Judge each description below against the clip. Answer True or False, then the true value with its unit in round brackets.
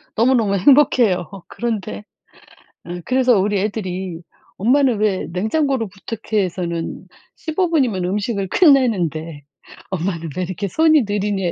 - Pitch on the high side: True (205 Hz)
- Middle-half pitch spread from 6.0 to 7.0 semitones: False (5.3 semitones)